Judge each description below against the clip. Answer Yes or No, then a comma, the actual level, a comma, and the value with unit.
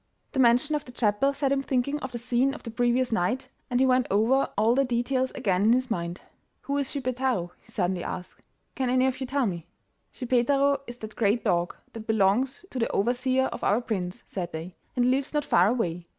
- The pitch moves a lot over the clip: No, average, 4.1 semitones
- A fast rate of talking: Yes, fast, 220 wpm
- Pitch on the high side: Yes, high, 245 Hz